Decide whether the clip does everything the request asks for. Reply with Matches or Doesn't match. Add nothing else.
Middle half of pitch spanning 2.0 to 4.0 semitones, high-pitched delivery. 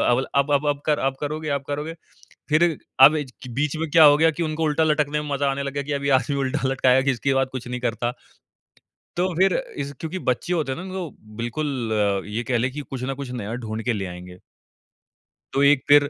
Doesn't match